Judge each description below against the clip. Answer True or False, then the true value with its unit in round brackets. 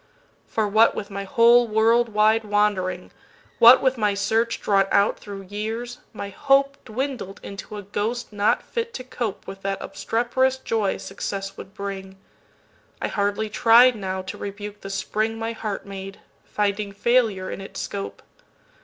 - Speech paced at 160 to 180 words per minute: False (140 wpm)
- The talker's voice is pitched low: False (210 Hz)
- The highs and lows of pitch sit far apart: False (2.7 semitones)